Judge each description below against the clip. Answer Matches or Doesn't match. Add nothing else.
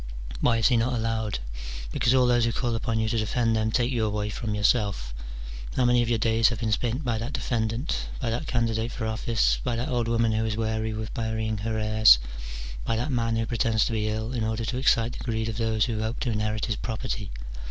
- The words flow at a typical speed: Doesn't match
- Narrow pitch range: Matches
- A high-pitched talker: Doesn't match